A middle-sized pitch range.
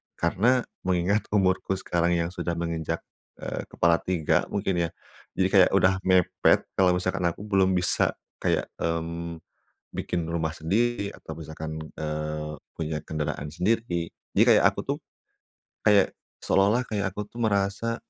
Yes: average, 3.1 semitones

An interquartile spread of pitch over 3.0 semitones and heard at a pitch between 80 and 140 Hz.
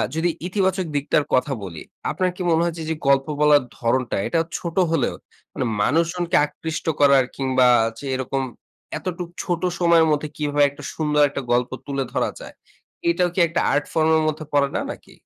No: average, 3.5 semitones; medium, 150 Hz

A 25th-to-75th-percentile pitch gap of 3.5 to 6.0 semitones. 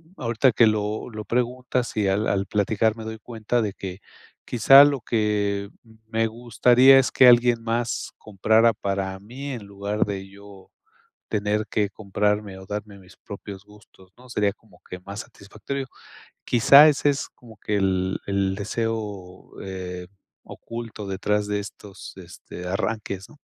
No: average, 2.9 semitones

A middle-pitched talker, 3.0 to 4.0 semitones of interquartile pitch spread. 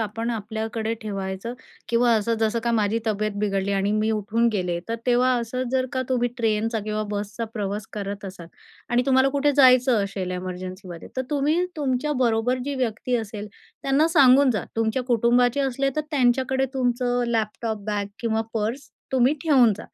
No: high, 230 Hz; average, 3.4 semitones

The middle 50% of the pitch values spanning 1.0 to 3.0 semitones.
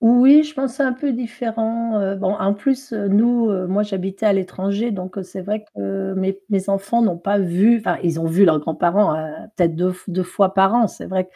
No: average, 3.7 semitones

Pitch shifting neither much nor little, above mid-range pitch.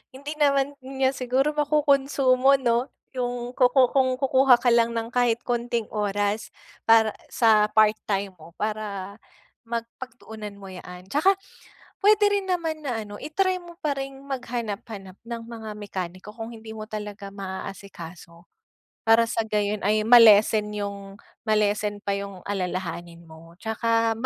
Yes: average, 4.2 semitones; high, 225 Hz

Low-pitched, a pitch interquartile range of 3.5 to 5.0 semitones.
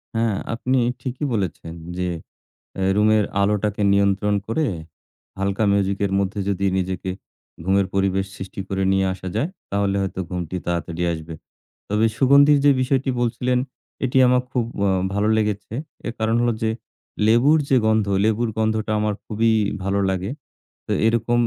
No: low, 105 Hz; average, 3.1 semitones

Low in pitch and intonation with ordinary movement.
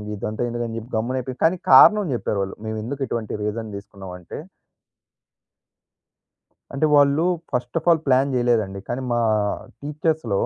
Yes: low, 120 Hz; average, 4.5 semitones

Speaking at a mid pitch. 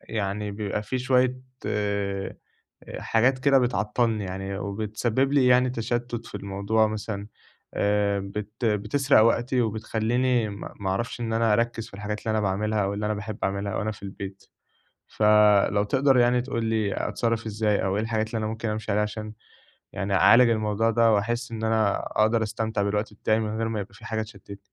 No: low, 110 Hz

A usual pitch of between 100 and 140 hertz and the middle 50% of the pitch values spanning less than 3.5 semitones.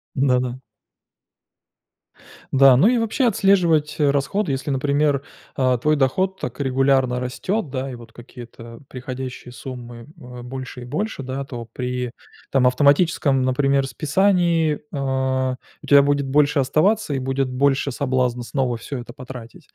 Yes: low, 135 Hz; narrow, 2.4 semitones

